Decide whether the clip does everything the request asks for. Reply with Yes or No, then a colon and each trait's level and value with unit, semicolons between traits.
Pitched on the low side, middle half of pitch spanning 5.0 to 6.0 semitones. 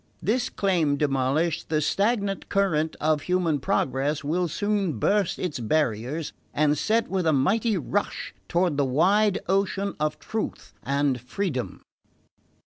No: medium, 165 Hz; wide, 5.5 semitones